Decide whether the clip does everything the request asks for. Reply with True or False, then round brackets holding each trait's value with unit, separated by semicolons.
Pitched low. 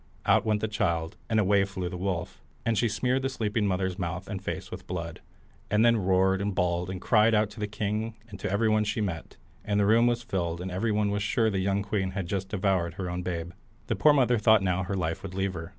True (100 Hz)